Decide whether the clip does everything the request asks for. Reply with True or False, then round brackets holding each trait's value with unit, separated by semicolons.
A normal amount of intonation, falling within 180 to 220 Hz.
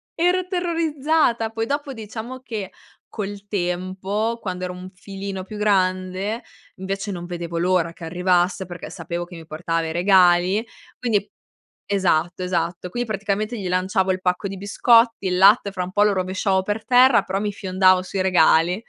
True (3.0 semitones; 190 Hz)